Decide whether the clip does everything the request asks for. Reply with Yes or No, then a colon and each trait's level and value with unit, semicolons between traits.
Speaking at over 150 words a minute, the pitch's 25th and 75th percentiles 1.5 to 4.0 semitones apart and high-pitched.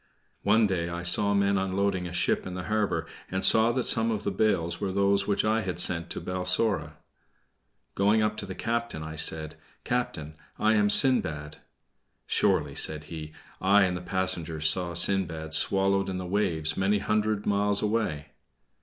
No: average, 170 wpm; average, 3.3 semitones; very low, 95 Hz